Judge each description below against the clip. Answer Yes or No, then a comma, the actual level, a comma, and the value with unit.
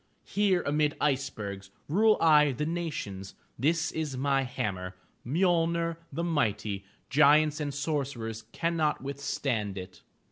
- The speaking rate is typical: No, slow, 115 wpm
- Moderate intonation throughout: No, wide, 6.2 semitones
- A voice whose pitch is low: No, medium, 145 Hz